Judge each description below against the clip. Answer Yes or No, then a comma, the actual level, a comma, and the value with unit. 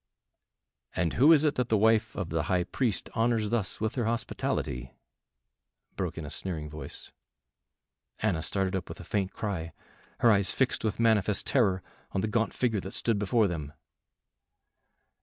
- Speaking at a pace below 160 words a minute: No, average, 165 wpm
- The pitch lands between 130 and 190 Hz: No, low, 105 Hz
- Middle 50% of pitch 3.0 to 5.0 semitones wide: Yes, average, 3.7 semitones